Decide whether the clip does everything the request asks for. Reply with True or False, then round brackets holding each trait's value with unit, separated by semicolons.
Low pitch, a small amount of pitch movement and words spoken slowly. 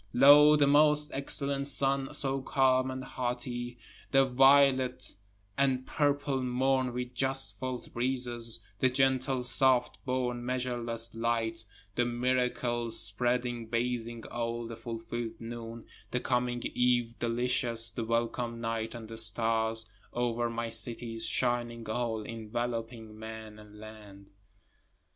True (120 Hz; 2.1 semitones; 120 wpm)